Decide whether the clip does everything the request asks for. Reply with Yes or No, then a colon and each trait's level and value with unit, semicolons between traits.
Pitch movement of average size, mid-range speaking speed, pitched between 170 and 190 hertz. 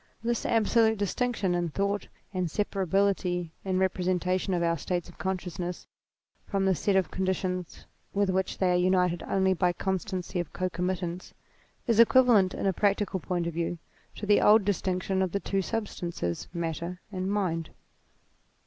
No: narrow, 2.0 semitones; average, 165 wpm; medium, 185 Hz